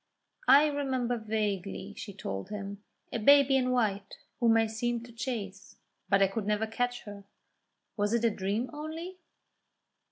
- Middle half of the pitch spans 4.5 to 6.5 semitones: No, average, 3.7 semitones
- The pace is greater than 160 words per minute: No, average, 155 wpm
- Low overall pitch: No, high, 225 Hz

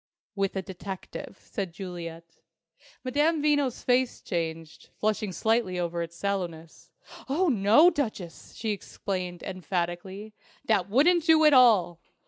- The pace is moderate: No, slow, 120 wpm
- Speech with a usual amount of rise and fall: No, wide, 6.3 semitones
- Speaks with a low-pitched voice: No, high, 195 Hz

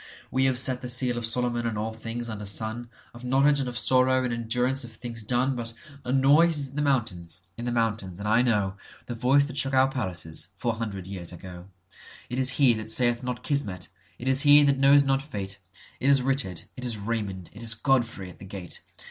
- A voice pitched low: Yes, low, 120 Hz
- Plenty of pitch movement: No, average, 4.0 semitones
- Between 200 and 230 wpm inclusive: Yes, fast, 205 wpm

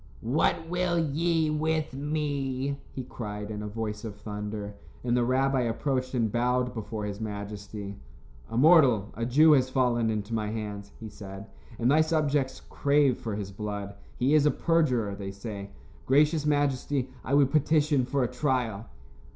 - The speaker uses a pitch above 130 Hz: No, low, 125 Hz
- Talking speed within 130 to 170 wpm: Yes, average, 165 wpm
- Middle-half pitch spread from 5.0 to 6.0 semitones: Yes, wide, 5.4 semitones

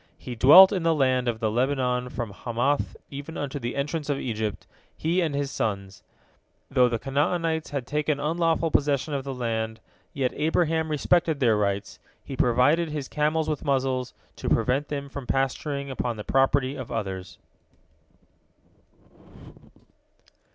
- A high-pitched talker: No, low, 135 Hz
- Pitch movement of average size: Yes, average, 3.6 semitones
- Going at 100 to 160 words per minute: Yes, average, 150 wpm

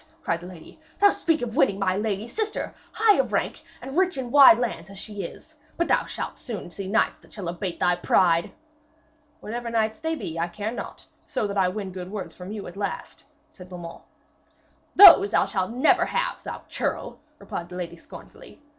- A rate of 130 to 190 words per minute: No, average, 200 wpm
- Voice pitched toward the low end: No, high, 205 Hz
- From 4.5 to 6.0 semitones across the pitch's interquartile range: Yes, average, 5.2 semitones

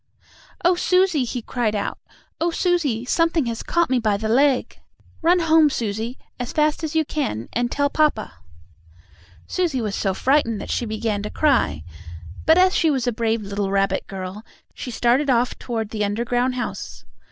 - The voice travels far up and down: Yes, wide, 5.9 semitones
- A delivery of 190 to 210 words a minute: No, average, 175 wpm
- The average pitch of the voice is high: Yes, high, 245 Hz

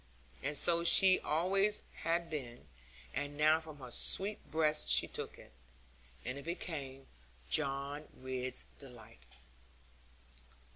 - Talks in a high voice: No, medium, 150 Hz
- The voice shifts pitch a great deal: No, average, 3.8 semitones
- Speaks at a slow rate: Yes, slow, 115 wpm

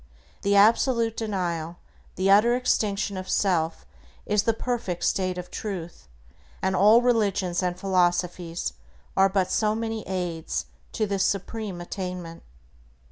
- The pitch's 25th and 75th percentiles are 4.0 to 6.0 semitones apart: No, average, 3.2 semitones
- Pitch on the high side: Yes, high, 195 Hz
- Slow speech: Yes, slow, 130 wpm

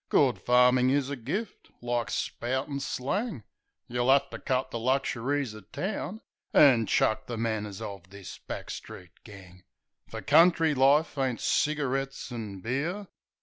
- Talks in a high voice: No, low, 130 Hz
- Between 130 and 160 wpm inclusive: Yes, average, 145 wpm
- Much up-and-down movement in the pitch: No, average, 3.8 semitones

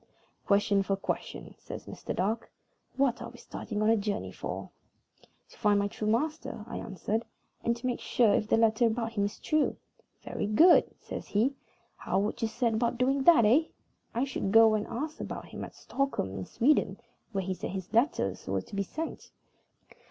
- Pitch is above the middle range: Yes, high, 225 Hz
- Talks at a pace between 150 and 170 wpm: No, average, 190 wpm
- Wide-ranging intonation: No, average, 3.5 semitones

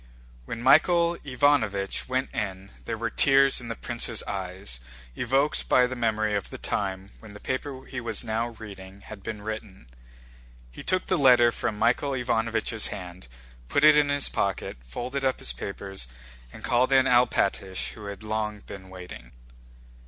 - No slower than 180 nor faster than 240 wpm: No, average, 165 wpm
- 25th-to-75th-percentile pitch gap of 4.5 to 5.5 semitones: Yes, average, 4.8 semitones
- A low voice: Yes, low, 110 Hz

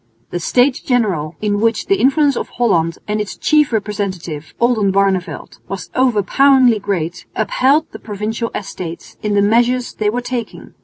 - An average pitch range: Yes, average, 4.1 semitones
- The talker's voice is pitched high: Yes, high, 215 Hz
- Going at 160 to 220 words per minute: No, average, 150 wpm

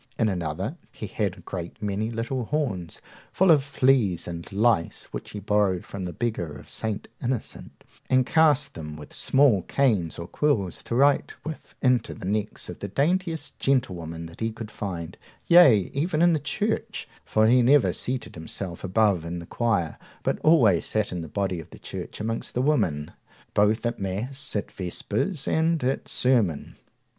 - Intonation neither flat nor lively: No, wide, 7.1 semitones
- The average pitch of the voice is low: Yes, low, 110 Hz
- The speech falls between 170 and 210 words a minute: Yes, average, 175 wpm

